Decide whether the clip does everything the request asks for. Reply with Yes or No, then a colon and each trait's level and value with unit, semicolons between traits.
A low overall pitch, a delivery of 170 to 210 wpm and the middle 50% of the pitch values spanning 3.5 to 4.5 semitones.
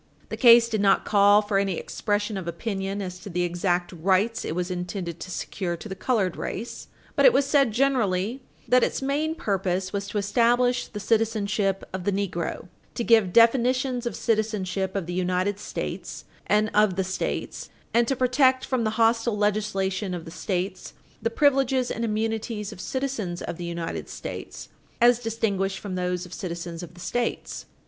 No: high, 205 Hz; average, 180 wpm; average, 4.1 semitones